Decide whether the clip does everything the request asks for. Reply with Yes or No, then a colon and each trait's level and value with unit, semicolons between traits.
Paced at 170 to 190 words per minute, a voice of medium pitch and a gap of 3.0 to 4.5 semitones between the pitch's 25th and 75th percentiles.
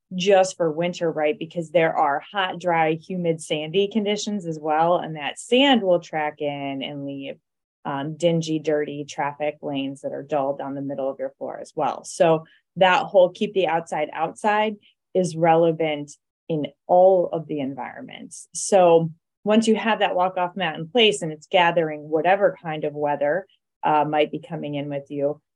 Yes: average, 180 wpm; medium, 165 Hz; average, 3.8 semitones